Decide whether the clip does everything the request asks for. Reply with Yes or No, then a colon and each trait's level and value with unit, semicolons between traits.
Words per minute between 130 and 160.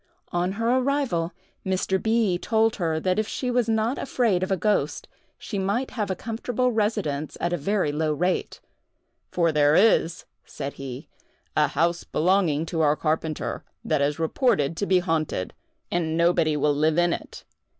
No: average, 170 wpm